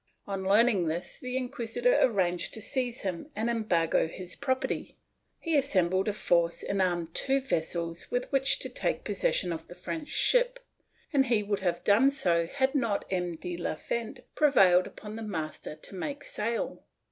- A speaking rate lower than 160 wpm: No, average, 170 wpm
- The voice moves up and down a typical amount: No, wide, 6.8 semitones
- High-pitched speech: Yes, high, 205 Hz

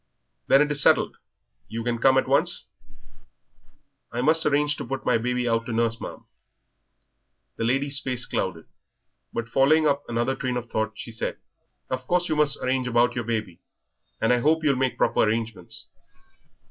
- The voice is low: Yes, low, 125 Hz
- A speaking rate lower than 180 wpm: Yes, average, 170 wpm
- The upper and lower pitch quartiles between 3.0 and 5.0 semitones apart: Yes, average, 3.3 semitones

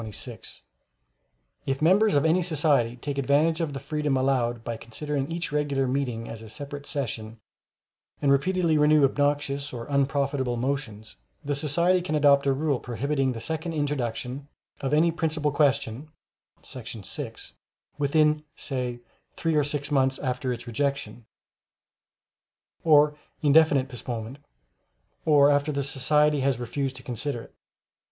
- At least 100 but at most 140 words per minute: Yes, slow, 135 wpm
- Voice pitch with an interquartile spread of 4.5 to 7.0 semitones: No, average, 2.9 semitones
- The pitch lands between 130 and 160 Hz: Yes, medium, 140 Hz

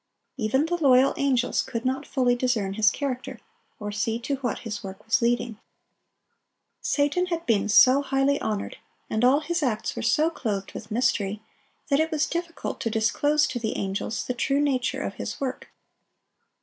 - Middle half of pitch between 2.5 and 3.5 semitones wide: No, average, 4.3 semitones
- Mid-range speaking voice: No, very high, 255 Hz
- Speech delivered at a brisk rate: No, average, 175 wpm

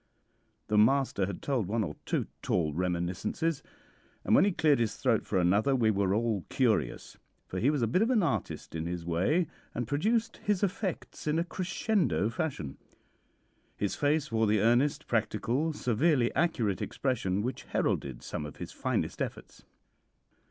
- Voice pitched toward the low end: Yes, low, 120 Hz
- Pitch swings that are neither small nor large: No, wide, 7.8 semitones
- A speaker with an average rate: Yes, average, 165 wpm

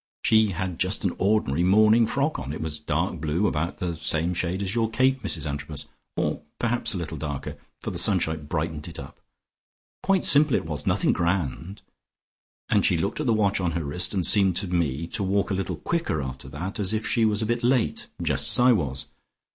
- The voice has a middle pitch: No, very low, 90 Hz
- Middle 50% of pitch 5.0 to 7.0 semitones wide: Yes, wide, 5.5 semitones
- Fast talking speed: Yes, fast, 215 wpm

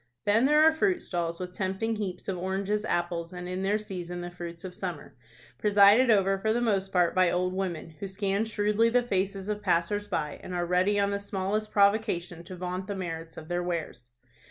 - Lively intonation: No, average, 2.7 semitones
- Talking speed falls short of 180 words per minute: No, fast, 205 wpm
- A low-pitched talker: No, high, 190 Hz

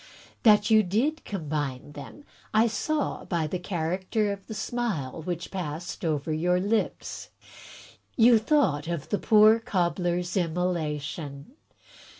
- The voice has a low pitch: No, medium, 180 Hz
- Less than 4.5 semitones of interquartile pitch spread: No, average, 5.3 semitones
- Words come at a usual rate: No, slow, 125 wpm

